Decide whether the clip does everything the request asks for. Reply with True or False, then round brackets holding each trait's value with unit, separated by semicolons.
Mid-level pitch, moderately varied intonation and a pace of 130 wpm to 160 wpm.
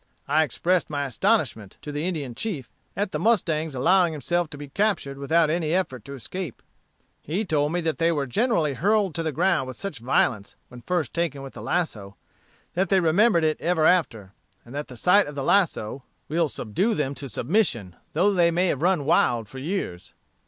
False (155 Hz; 4.9 semitones; 195 wpm)